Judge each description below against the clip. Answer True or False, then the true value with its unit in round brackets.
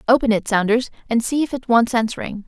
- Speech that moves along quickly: True (220 wpm)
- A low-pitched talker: False (235 Hz)